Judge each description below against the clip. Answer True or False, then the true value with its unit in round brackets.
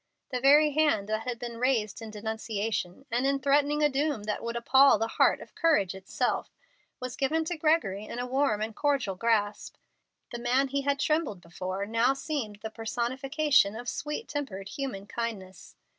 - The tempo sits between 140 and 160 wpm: False (175 wpm)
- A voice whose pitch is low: False (245 Hz)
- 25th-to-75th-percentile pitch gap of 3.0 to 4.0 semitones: False (4.7 semitones)